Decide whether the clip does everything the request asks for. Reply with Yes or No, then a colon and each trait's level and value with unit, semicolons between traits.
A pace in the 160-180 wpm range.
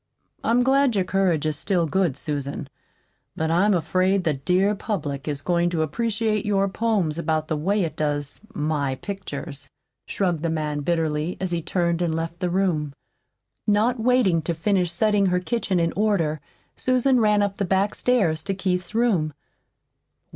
Yes: average, 165 wpm